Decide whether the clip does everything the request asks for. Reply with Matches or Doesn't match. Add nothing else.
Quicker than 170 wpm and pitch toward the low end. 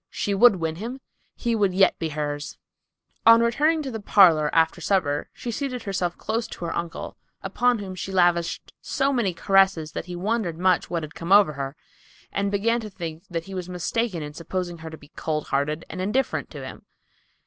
Doesn't match